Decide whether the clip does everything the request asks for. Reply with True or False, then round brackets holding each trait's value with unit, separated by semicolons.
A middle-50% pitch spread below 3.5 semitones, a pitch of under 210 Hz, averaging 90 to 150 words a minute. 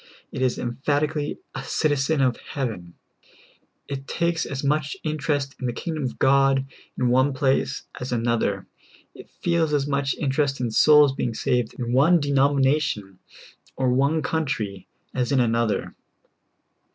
True (2.9 semitones; 135 Hz; 140 wpm)